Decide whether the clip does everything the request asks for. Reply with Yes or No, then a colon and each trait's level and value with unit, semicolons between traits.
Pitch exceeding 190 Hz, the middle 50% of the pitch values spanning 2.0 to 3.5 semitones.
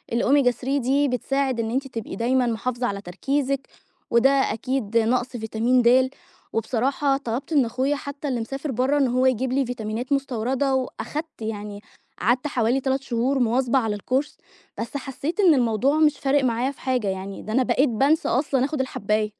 Yes: very high, 255 Hz; average, 3.0 semitones